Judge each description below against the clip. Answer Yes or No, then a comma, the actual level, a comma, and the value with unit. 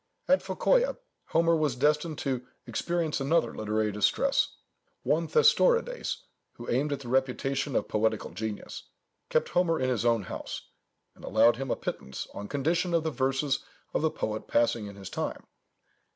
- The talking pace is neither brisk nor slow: Yes, average, 160 wpm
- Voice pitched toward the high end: No, low, 135 Hz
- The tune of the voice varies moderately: No, wide, 6.1 semitones